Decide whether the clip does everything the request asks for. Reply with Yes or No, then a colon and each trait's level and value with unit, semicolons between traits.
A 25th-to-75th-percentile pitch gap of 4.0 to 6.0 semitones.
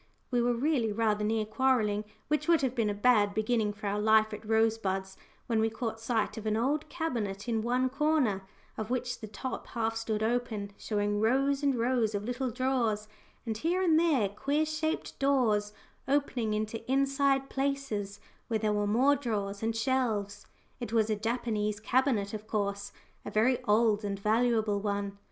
No: average, 3.6 semitones